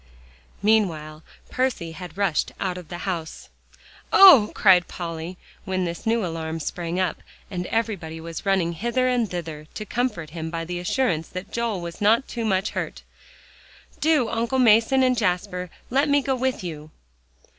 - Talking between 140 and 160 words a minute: Yes, average, 155 wpm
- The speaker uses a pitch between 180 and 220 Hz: Yes, medium, 185 Hz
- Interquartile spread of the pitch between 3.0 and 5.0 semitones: No, wide, 5.5 semitones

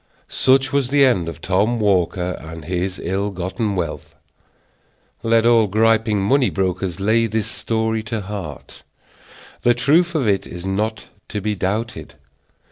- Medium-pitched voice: No, low, 105 Hz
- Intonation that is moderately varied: Yes, average, 3.6 semitones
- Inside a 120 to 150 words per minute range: Yes, average, 145 wpm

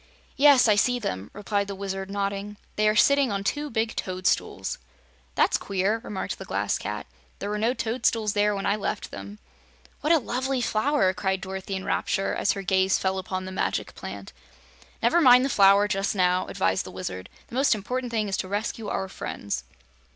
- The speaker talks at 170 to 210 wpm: Yes, average, 190 wpm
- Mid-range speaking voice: No, high, 200 Hz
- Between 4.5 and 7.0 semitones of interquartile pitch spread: No, average, 3.2 semitones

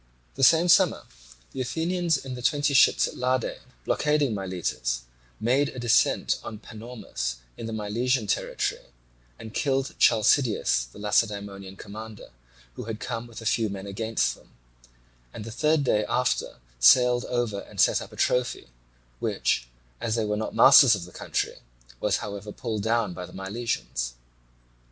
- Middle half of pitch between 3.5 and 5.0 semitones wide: Yes, average, 3.9 semitones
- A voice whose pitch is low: Yes, low, 110 Hz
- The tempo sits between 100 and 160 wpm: Yes, average, 155 wpm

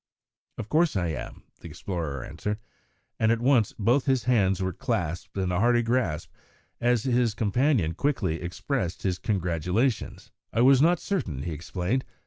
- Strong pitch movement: Yes, wide, 6.1 semitones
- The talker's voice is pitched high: No, low, 105 Hz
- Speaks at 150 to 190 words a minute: Yes, average, 155 wpm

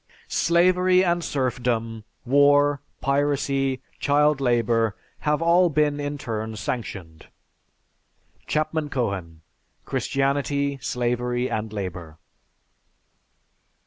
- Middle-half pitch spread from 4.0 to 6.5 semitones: Yes, average, 4.3 semitones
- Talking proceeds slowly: Yes, slow, 80 wpm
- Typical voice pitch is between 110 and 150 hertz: Yes, low, 135 Hz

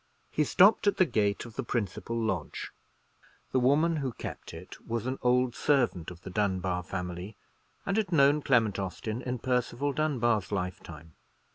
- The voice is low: Yes, low, 115 Hz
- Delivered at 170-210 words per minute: No, average, 160 wpm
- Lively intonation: Yes, wide, 6.3 semitones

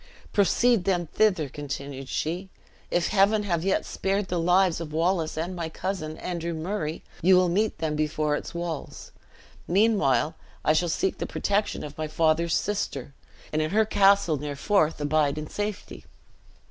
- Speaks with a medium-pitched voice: Yes, medium, 170 Hz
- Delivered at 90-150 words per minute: No, average, 165 wpm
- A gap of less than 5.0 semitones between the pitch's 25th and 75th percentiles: Yes, average, 4.0 semitones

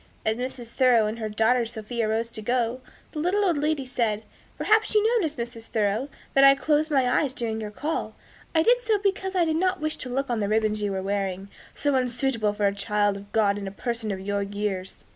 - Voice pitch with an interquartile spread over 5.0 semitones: Yes, wide, 5.5 semitones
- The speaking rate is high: Yes, fast, 225 wpm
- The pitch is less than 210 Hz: No, high, 235 Hz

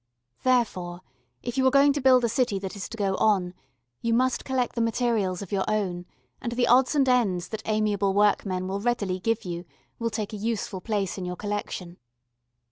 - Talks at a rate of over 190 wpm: Yes, average, 200 wpm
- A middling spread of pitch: Yes, average, 4.1 semitones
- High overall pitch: Yes, high, 215 Hz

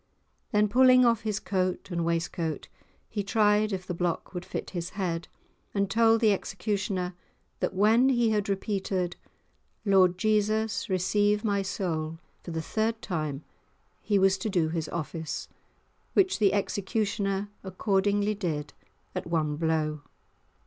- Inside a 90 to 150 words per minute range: Yes, average, 140 wpm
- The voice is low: No, high, 195 Hz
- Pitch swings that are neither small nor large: Yes, average, 3.4 semitones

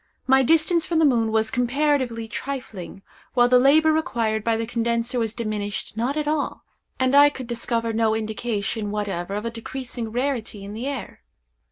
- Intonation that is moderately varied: Yes, average, 3.4 semitones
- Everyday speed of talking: Yes, average, 175 wpm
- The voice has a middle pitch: No, high, 235 Hz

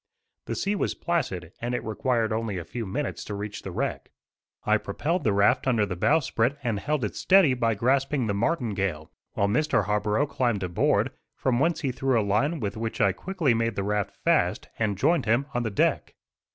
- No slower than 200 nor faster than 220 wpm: Yes, fast, 205 wpm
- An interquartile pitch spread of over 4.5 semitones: Yes, average, 5.1 semitones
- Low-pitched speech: Yes, low, 115 Hz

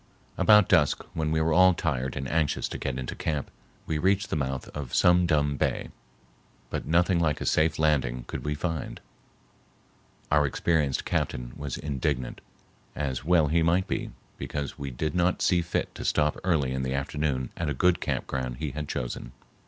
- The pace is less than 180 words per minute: No, average, 185 wpm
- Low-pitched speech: Yes, very low, 75 Hz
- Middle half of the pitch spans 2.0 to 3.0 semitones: No, average, 3.6 semitones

